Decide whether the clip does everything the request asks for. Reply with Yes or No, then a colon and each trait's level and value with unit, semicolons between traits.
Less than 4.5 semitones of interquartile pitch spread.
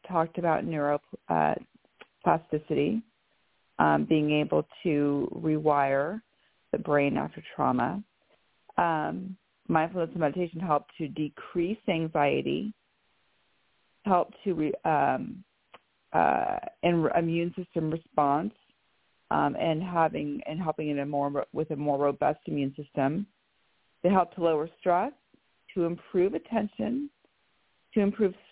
Yes: average, 3.8 semitones